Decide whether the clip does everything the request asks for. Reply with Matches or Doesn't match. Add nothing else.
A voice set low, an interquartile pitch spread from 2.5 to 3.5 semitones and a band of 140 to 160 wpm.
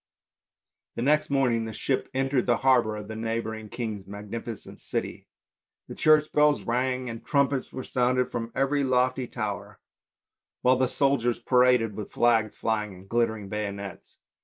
Matches